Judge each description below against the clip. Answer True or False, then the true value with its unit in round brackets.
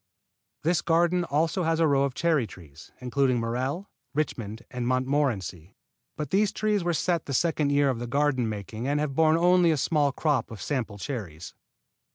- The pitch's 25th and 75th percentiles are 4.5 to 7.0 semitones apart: True (5.3 semitones)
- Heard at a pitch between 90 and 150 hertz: True (140 Hz)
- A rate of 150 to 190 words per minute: True (180 wpm)